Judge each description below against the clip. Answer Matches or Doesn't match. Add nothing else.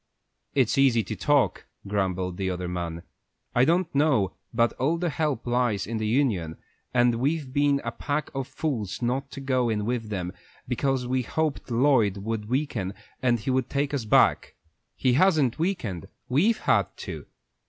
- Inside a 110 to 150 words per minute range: Doesn't match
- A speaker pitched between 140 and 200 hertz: Doesn't match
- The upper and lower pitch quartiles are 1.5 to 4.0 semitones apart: Doesn't match